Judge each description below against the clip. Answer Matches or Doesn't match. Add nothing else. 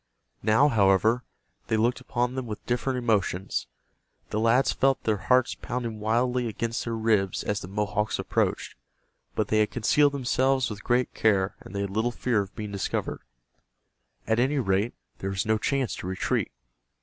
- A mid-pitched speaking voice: Doesn't match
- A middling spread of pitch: Matches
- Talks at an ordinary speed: Matches